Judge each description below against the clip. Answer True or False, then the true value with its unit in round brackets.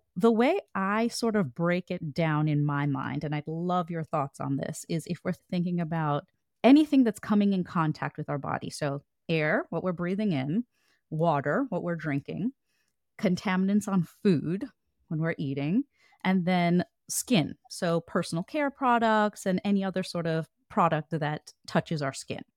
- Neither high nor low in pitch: True (175 Hz)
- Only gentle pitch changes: False (4.2 semitones)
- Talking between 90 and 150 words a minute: False (170 wpm)